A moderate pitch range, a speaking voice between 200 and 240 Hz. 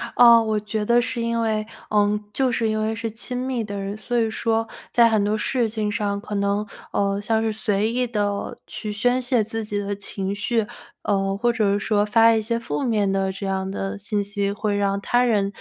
No: narrow, 2.1 semitones; high, 215 Hz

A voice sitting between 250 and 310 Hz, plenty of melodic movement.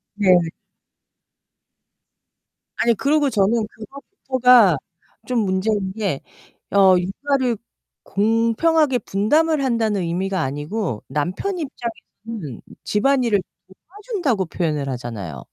No: high, 215 Hz; wide, 5.8 semitones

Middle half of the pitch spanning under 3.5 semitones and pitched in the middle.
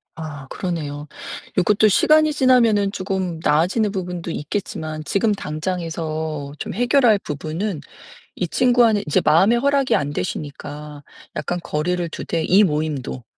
No: wide, 5.5 semitones; medium, 175 Hz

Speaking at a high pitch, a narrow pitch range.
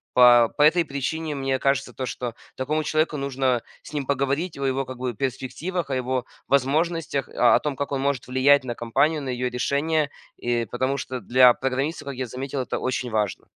No: low, 135 Hz; narrow, 2.1 semitones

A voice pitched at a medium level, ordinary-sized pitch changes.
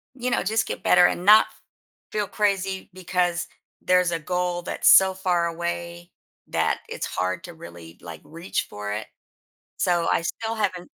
No: medium, 175 Hz; narrow, 2.1 semitones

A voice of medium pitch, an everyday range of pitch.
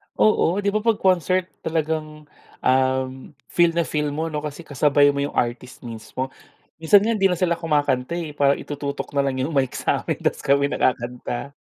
Yes: medium, 150 Hz; average, 4.1 semitones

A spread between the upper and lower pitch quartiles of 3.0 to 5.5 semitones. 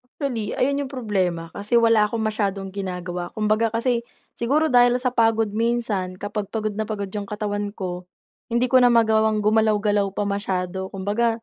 No: narrow, 2.6 semitones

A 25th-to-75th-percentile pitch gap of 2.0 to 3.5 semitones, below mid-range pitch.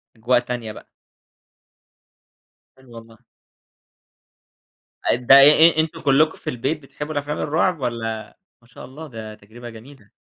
No: average, 4.3 semitones; low, 125 Hz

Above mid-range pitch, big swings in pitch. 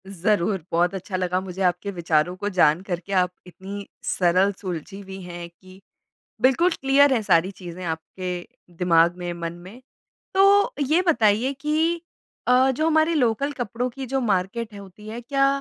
Yes: high, 195 Hz; wide, 6.4 semitones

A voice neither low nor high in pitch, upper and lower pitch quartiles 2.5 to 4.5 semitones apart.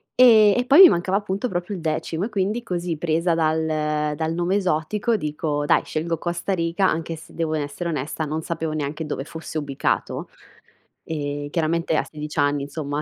Yes: medium, 160 Hz; average, 2.9 semitones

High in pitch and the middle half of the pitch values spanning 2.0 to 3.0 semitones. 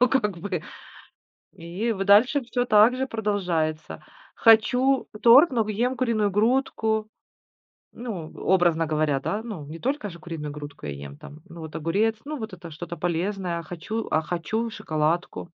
No: high, 200 Hz; wide, 5.6 semitones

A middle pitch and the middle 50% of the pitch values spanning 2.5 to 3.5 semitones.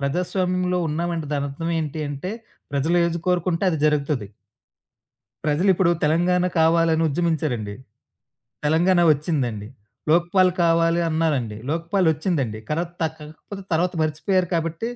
Yes: medium, 165 Hz; average, 2.8 semitones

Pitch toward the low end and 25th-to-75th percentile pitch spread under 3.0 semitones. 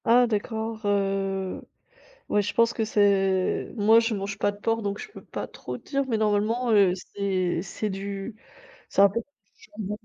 No: high, 205 Hz; narrow, 2.5 semitones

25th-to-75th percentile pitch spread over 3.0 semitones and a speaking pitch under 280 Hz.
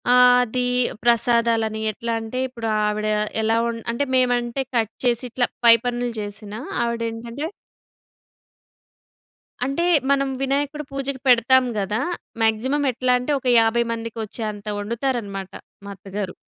No: narrow, 2.6 semitones; high, 235 Hz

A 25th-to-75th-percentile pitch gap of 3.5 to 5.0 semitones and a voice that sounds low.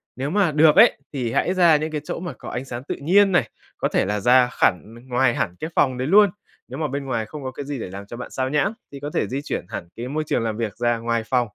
Yes: average, 4.5 semitones; low, 130 Hz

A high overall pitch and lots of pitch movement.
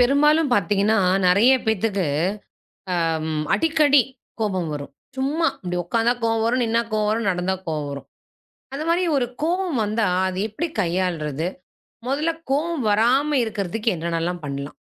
Yes: high, 220 Hz; wide, 7.3 semitones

